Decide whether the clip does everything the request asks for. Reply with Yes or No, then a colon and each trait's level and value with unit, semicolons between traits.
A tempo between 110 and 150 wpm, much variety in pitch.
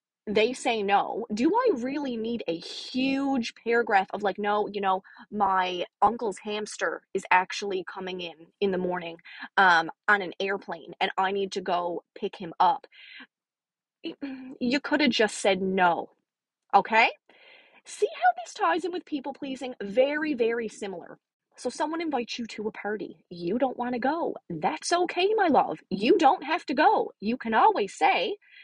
No: average, 170 wpm; wide, 7.6 semitones